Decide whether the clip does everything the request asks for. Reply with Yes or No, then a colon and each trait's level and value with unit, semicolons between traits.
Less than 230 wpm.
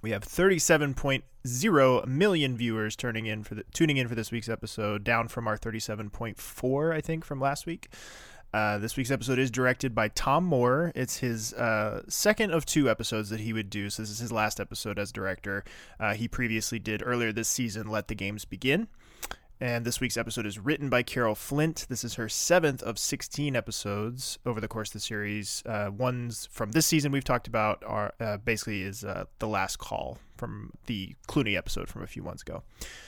Yes: fast, 205 wpm